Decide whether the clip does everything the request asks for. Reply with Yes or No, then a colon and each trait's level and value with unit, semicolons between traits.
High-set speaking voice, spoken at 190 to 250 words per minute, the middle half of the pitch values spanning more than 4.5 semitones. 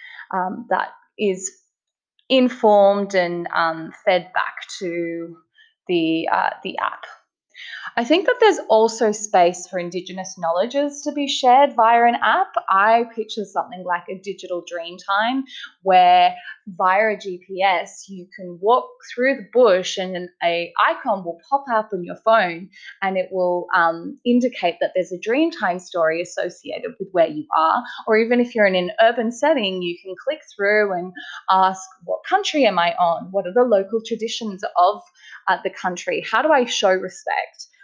No: high, 200 Hz; average, 165 wpm; average, 5.2 semitones